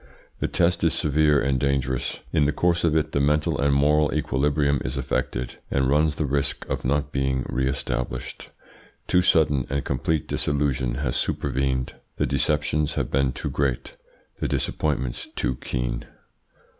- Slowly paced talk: No, average, 155 wpm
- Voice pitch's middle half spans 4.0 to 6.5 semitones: No, narrow, 2.4 semitones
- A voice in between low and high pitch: No, very low, 70 Hz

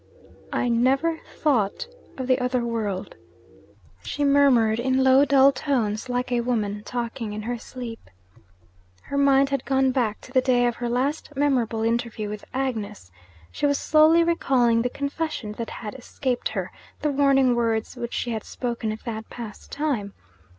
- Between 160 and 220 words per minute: Yes, average, 165 wpm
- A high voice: Yes, high, 245 Hz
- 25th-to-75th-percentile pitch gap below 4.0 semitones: Yes, average, 3.1 semitones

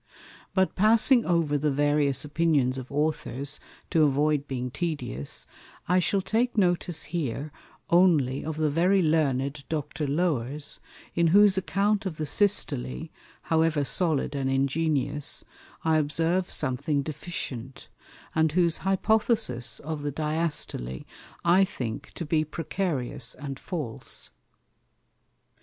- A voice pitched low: No, medium, 155 Hz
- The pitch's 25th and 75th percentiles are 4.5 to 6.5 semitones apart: No, average, 3.9 semitones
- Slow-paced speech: Yes, slow, 120 wpm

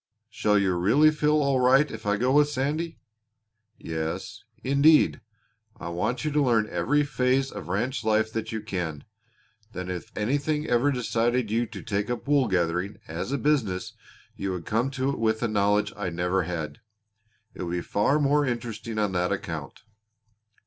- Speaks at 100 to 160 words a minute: No, average, 175 wpm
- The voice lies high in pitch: No, low, 115 Hz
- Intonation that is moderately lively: No, wide, 6.3 semitones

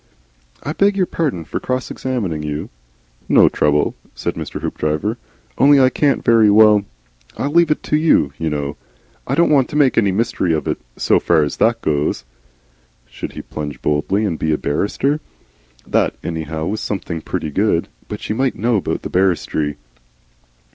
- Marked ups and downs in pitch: Yes, wide, 8.9 semitones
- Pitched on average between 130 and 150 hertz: No, low, 100 Hz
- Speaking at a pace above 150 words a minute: Yes, average, 170 wpm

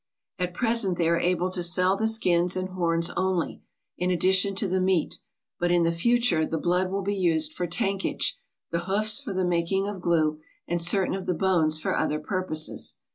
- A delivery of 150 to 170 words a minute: No, average, 195 wpm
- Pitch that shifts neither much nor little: No, narrow, 2.3 semitones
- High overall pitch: No, medium, 180 Hz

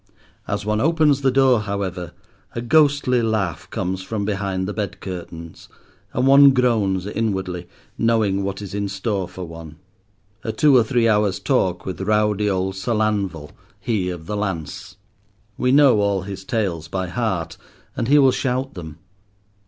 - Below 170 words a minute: Yes, average, 160 wpm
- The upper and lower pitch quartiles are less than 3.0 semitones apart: No, average, 4.0 semitones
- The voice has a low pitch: Yes, low, 100 Hz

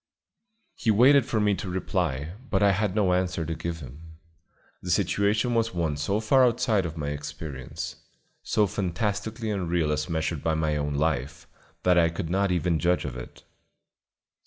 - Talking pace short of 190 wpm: Yes, average, 170 wpm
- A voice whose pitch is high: No, very low, 90 Hz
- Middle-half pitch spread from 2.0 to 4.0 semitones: No, average, 4.8 semitones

